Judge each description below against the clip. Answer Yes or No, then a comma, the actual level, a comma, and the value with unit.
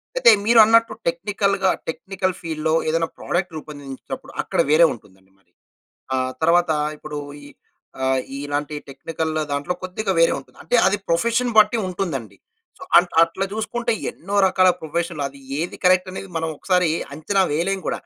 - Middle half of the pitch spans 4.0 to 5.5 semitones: Yes, average, 4.3 semitones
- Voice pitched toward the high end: No, medium, 170 Hz